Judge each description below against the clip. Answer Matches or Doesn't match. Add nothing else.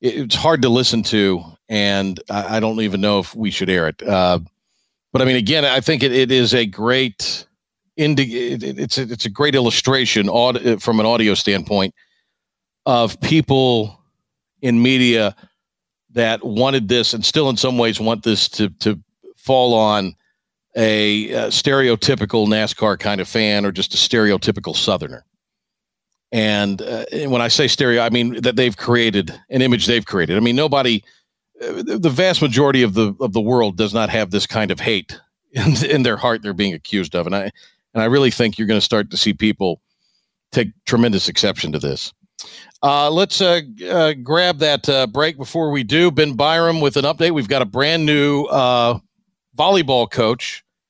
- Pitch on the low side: Matches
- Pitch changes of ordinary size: Matches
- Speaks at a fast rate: Doesn't match